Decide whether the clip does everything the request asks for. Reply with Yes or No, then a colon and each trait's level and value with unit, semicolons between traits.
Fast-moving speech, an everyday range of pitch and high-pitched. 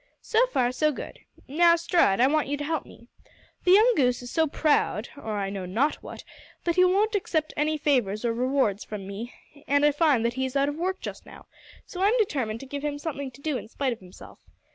Yes: fast, 230 wpm; average, 5.0 semitones; very high, 285 Hz